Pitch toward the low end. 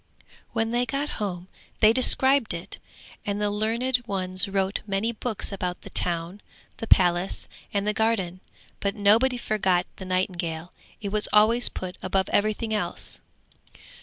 No: high, 205 Hz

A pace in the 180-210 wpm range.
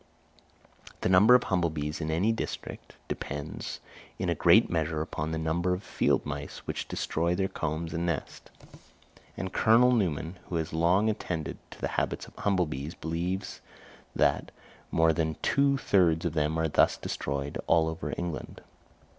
No: average, 165 wpm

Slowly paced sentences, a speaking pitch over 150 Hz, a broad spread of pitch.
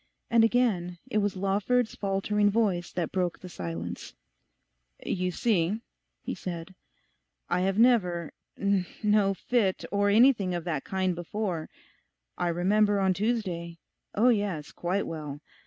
No: slow, 130 wpm; high, 190 Hz; average, 3.2 semitones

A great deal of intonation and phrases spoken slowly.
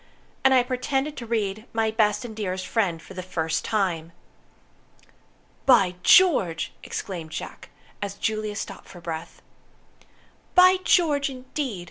Yes: wide, 5.7 semitones; slow, 130 wpm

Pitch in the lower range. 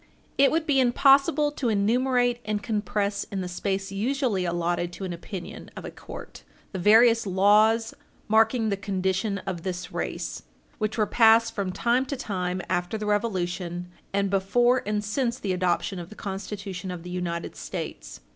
No: high, 205 Hz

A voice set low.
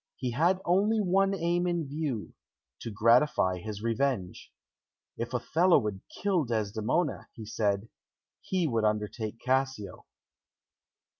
Yes: low, 125 Hz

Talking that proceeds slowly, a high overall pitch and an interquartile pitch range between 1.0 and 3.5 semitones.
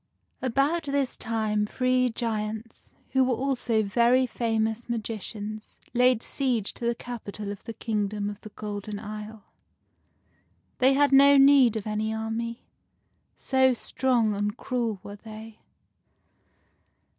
Yes: slow, 125 wpm; high, 225 Hz; average, 3.0 semitones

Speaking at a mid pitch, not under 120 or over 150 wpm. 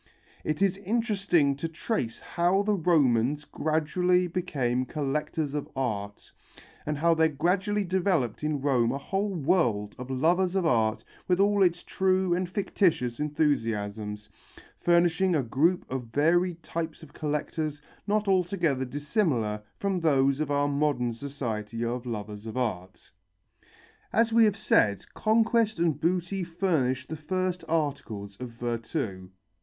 Yes: medium, 155 Hz; average, 140 wpm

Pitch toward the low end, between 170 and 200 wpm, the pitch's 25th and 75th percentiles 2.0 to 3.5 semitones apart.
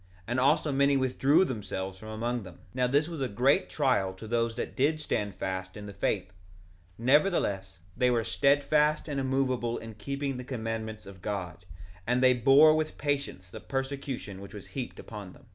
No: low, 125 Hz; average, 185 wpm; average, 5.2 semitones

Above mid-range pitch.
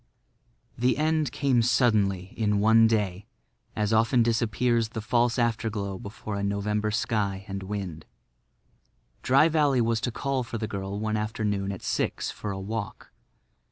No: low, 110 Hz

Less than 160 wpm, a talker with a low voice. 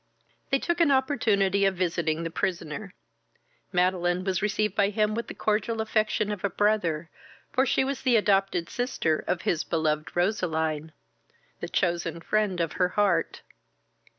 No: average, 150 wpm; high, 195 Hz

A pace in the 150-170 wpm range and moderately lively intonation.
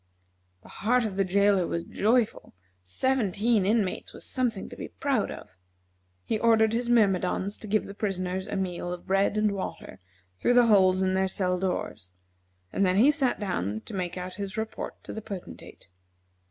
No: average, 180 wpm; average, 3.1 semitones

